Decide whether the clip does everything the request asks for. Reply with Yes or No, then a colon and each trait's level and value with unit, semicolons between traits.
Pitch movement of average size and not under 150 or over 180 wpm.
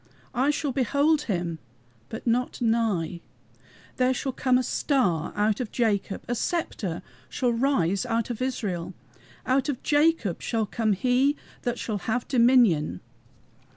No: average, 4.3 semitones; average, 140 wpm